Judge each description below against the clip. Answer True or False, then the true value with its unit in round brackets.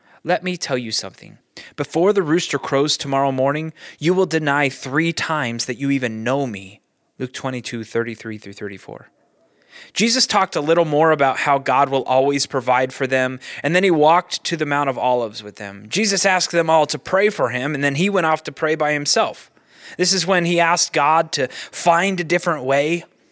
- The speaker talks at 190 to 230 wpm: True (200 wpm)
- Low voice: False (145 Hz)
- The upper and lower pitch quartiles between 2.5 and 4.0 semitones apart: False (4.8 semitones)